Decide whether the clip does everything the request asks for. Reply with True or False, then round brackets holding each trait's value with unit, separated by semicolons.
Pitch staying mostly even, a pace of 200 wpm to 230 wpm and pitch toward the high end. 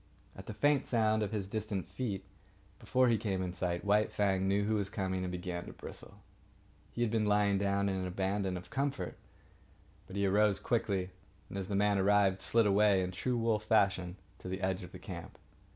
False (2.2 semitones; 205 wpm; 100 Hz)